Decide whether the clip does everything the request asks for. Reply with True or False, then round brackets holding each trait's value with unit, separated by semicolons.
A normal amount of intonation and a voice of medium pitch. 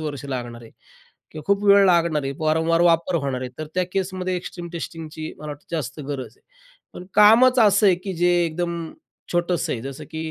True (3.9 semitones; 165 Hz)